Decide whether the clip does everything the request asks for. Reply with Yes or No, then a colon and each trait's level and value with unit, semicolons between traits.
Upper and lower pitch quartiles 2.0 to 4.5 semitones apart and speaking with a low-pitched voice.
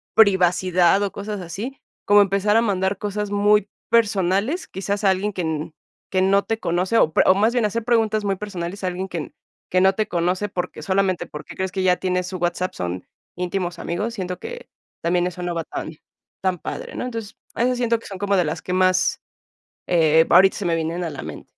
No: narrow, 2.6 semitones; high, 190 Hz